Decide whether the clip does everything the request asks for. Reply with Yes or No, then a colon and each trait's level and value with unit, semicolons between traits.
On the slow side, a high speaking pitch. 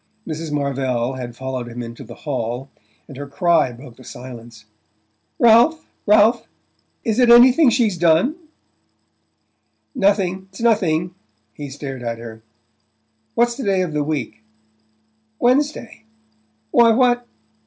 No: slow, 125 wpm; medium, 160 Hz